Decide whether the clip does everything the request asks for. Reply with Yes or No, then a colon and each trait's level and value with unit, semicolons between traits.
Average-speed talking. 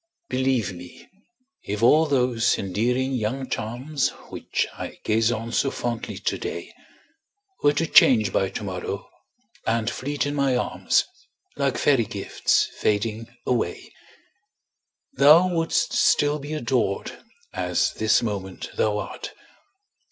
No: slow, 120 wpm